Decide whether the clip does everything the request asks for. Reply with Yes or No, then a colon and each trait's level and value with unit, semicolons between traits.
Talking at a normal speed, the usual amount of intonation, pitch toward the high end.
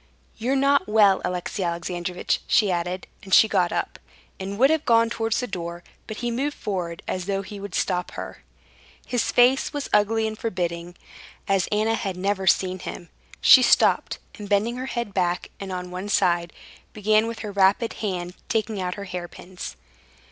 Yes: average, 175 wpm; average, 3.8 semitones; high, 200 Hz